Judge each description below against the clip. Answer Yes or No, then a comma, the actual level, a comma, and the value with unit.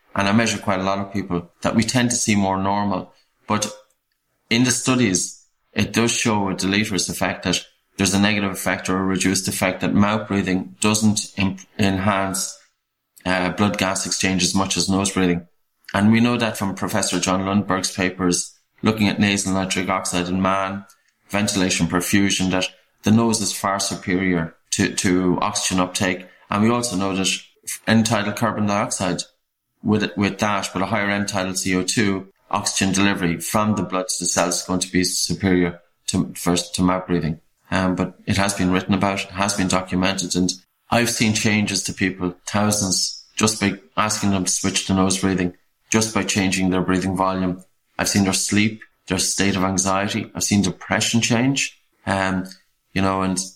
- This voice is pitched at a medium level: No, very low, 95 Hz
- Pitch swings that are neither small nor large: No, narrow, 1.9 semitones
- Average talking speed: Yes, average, 180 wpm